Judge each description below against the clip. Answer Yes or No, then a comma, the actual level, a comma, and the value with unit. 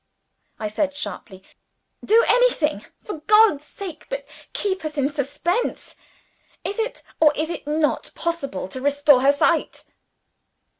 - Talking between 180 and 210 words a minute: No, slow, 135 wpm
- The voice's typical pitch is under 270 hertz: No, very high, 300 Hz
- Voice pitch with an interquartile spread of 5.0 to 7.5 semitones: Yes, wide, 5.4 semitones